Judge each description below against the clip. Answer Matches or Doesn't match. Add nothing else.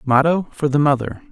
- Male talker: Matches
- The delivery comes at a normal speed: Matches